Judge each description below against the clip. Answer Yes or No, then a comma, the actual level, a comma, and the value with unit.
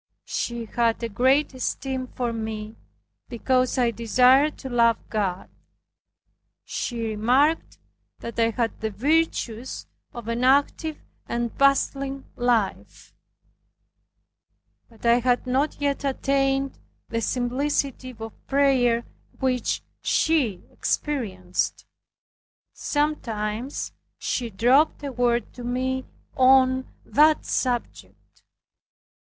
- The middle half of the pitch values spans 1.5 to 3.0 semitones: Yes, average, 2.7 semitones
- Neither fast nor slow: No, slow, 100 wpm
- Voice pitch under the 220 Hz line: No, very high, 250 Hz